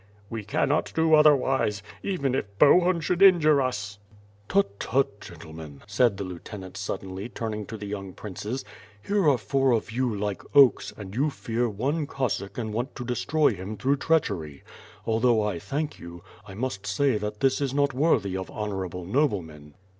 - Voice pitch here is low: Yes, low, 110 Hz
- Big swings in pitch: Yes, wide, 5.8 semitones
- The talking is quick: No, average, 175 wpm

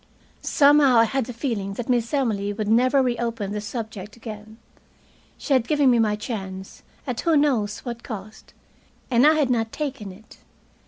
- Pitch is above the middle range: Yes, high, 230 Hz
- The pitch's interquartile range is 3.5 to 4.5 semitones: Yes, average, 3.8 semitones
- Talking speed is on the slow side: No, average, 170 wpm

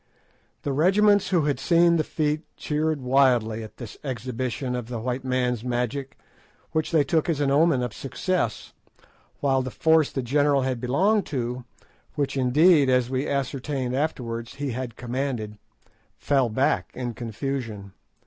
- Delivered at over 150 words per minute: No, average, 145 wpm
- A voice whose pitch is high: No, low, 130 Hz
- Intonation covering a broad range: No, average, 3.3 semitones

